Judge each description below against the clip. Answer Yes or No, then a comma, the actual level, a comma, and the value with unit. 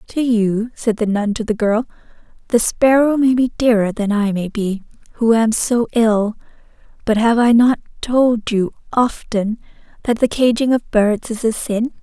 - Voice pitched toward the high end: Yes, high, 225 Hz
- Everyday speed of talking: Yes, average, 180 wpm